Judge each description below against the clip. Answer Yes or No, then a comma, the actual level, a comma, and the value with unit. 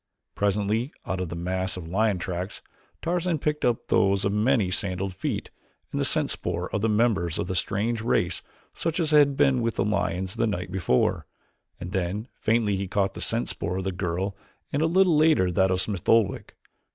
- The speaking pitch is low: Yes, low, 100 Hz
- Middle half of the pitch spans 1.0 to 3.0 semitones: No, average, 4.1 semitones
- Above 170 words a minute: Yes, average, 200 wpm